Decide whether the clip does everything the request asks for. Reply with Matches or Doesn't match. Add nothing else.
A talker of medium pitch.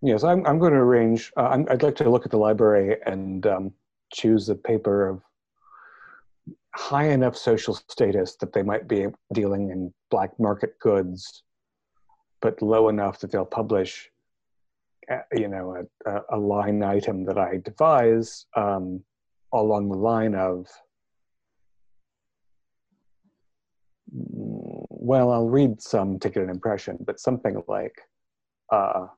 Doesn't match